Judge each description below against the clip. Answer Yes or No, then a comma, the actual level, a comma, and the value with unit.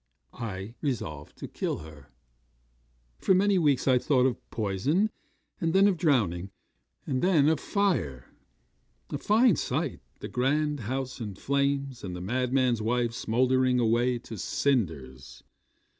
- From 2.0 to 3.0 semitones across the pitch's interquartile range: No, wide, 5.4 semitones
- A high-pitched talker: No, low, 125 Hz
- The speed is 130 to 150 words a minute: Yes, slow, 135 wpm